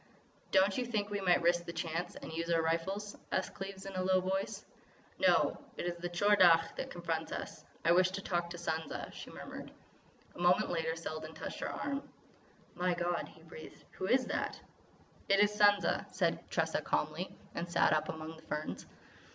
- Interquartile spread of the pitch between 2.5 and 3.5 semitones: Yes, average, 2.8 semitones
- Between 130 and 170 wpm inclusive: No, average, 190 wpm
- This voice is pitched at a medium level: Yes, medium, 175 Hz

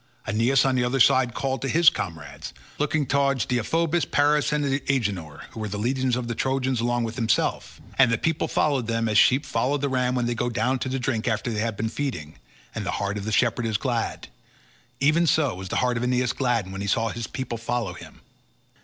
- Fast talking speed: Yes, fast, 215 wpm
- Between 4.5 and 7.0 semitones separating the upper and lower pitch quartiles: No, average, 3.2 semitones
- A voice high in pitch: No, low, 125 Hz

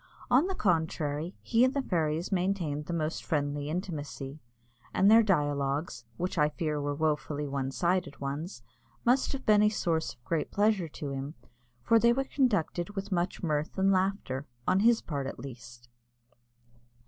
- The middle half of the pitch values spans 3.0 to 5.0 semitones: No, wide, 5.4 semitones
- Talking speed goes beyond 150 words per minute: Yes, average, 165 wpm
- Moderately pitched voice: Yes, medium, 160 Hz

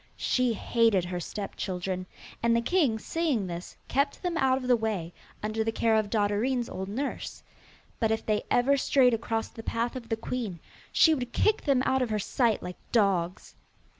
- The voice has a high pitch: Yes, high, 225 Hz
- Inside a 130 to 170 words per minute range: No, average, 190 wpm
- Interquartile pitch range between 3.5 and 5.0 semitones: Yes, average, 3.8 semitones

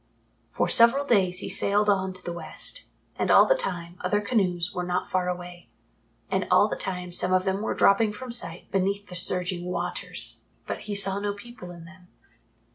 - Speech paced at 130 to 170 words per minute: No, average, 195 wpm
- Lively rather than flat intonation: No, narrow, 2.4 semitones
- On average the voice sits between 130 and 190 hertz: Yes, medium, 185 Hz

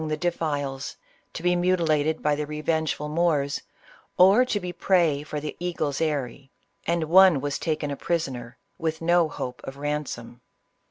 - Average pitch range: Yes, average, 3.1 semitones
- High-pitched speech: No, medium, 155 Hz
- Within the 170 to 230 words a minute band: No, average, 155 wpm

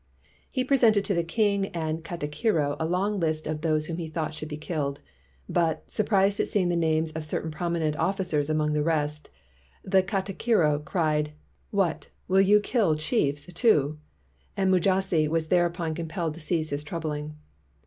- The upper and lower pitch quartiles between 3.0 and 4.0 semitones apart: Yes, average, 3.7 semitones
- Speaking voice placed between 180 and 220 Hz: No, medium, 165 Hz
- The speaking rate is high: No, average, 170 wpm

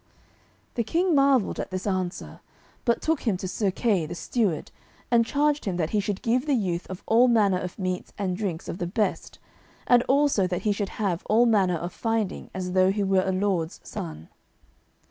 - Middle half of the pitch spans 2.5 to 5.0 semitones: Yes, average, 4.2 semitones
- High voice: Yes, high, 200 Hz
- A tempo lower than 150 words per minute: No, average, 200 wpm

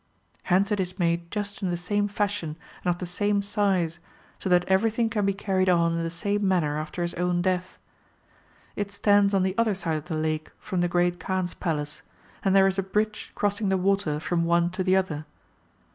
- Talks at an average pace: No, fast, 215 wpm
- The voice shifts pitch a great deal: No, average, 2.7 semitones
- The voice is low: No, medium, 185 Hz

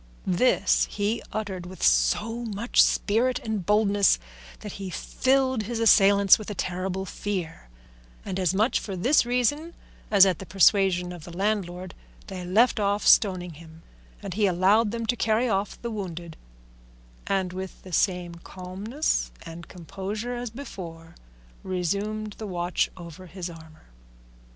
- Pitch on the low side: No, high, 195 Hz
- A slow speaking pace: No, average, 145 wpm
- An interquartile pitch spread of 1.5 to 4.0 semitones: Yes, average, 3.4 semitones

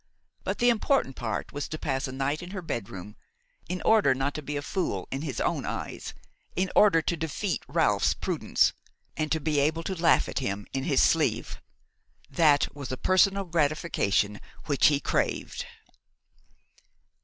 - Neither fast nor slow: Yes, average, 165 wpm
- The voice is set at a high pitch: No, medium, 150 Hz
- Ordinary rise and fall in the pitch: Yes, average, 4.6 semitones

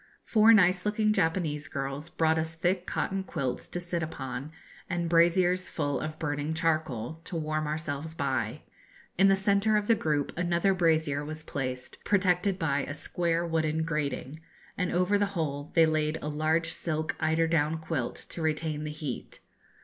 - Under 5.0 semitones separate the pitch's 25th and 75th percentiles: Yes, average, 2.8 semitones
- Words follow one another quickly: No, average, 165 wpm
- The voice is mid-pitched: Yes, medium, 160 Hz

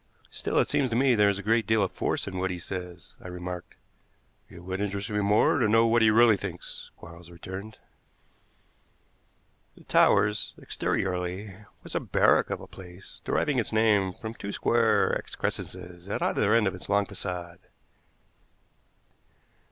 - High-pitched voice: No, low, 100 Hz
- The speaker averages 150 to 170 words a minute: Yes, average, 165 wpm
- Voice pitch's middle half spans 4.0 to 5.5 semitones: No, average, 3.3 semitones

